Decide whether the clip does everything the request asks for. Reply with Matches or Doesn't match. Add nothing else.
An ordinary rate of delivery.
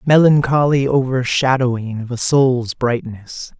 Doesn't match